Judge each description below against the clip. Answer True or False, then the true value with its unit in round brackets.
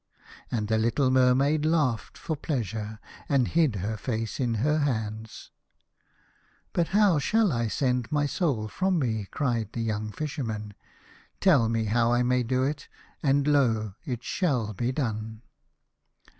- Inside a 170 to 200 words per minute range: False (155 wpm)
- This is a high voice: False (125 Hz)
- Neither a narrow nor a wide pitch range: True (4.7 semitones)